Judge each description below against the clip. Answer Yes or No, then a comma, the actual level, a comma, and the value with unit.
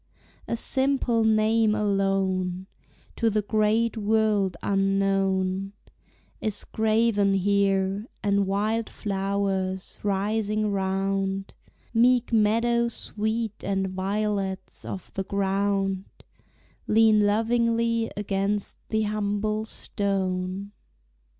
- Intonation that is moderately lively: No, narrow, 2.0 semitones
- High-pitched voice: Yes, high, 205 Hz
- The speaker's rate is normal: No, slow, 85 wpm